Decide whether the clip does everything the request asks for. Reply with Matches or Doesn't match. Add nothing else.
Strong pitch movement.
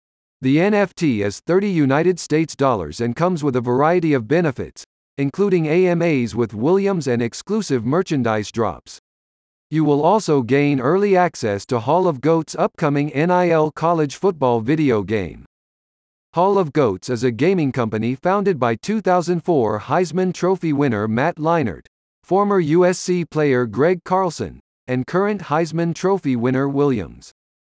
Matches